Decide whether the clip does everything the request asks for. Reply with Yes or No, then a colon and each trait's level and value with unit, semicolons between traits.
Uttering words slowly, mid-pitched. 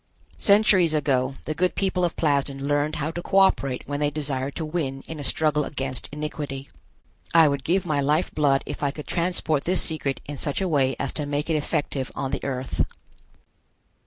No: average, 195 wpm; medium, 145 Hz